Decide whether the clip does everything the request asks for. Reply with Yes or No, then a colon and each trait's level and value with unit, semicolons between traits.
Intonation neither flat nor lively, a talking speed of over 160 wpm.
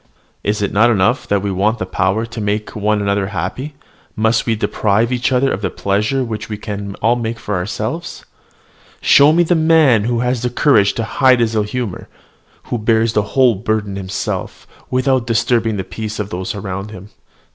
Yes: average, 3.2 semitones; average, 190 wpm